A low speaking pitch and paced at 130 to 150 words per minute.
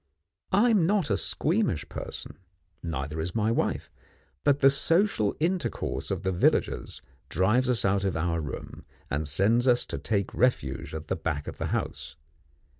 No: low, 100 Hz; average, 165 wpm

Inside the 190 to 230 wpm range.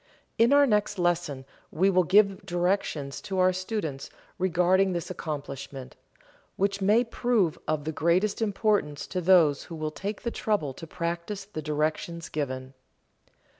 No: average, 145 wpm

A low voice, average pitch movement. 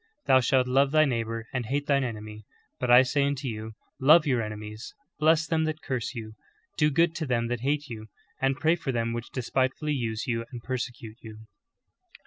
Yes: low, 125 Hz; average, 3.8 semitones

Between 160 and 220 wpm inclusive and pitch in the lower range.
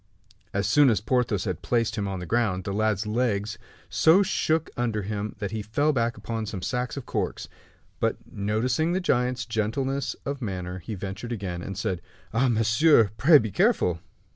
Yes: average, 180 wpm; low, 110 Hz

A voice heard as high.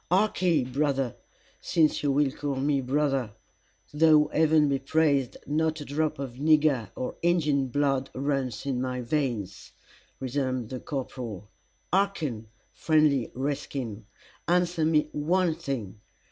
No: medium, 140 Hz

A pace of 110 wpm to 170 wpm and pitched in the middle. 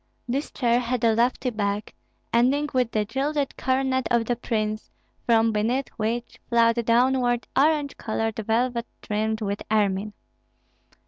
No: slow, 135 wpm; high, 235 Hz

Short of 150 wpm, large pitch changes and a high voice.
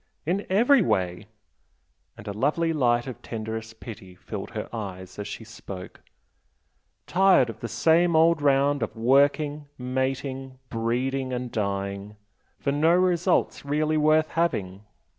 No: slow, 135 wpm; wide, 6.0 semitones; low, 130 Hz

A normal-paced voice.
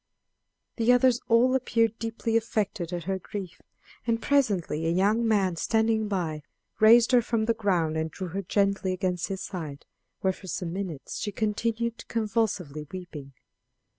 Yes: average, 155 wpm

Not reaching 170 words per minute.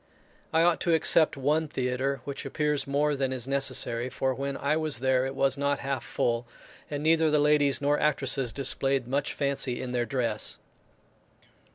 No: average, 175 wpm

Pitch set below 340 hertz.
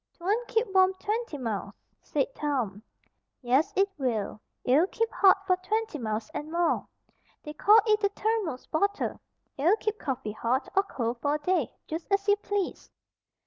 No: very high, 345 Hz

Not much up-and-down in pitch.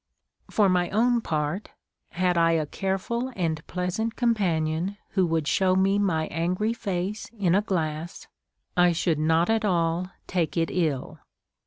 No: average, 3.5 semitones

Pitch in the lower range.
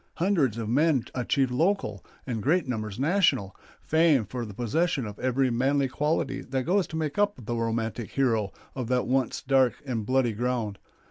Yes: low, 130 Hz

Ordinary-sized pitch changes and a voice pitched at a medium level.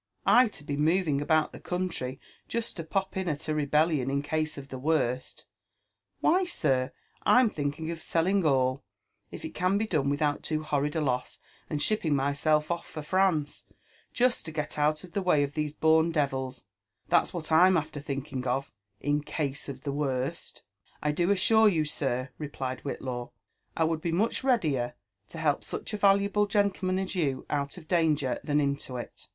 Yes: average, 4.1 semitones; medium, 155 Hz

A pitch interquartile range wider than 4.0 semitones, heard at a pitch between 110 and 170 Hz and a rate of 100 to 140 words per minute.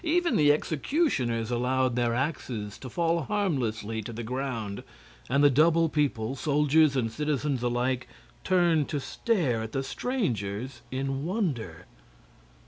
Yes: average, 4.9 semitones; low, 135 Hz; slow, 135 wpm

